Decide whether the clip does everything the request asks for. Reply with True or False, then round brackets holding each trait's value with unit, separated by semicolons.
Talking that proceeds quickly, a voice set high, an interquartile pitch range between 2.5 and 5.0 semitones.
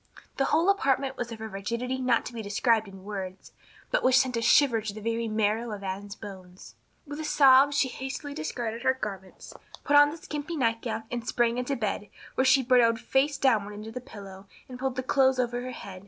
True (215 wpm; 240 Hz; 3.8 semitones)